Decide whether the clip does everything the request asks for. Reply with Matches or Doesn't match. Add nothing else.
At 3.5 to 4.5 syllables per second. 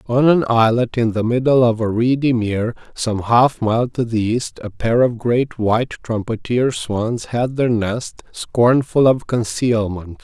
Matches